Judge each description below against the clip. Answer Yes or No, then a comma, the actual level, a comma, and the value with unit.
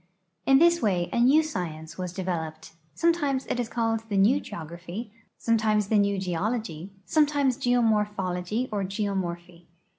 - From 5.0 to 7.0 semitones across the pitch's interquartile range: Yes, wide, 5.4 semitones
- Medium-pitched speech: No, high, 210 Hz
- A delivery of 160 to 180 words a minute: No, average, 145 wpm